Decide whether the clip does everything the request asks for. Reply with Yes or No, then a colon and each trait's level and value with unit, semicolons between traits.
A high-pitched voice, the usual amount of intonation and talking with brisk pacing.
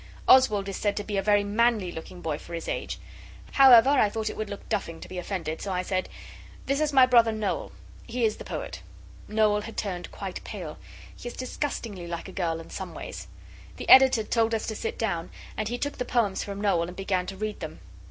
Yes: high, 210 Hz; average, 3.9 semitones; fast, 225 wpm